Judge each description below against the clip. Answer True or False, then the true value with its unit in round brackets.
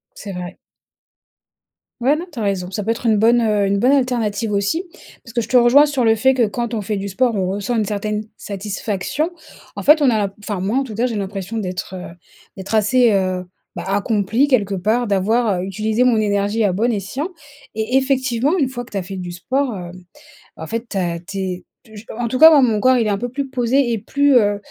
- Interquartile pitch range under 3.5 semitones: False (3.9 semitones)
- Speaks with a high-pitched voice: True (220 Hz)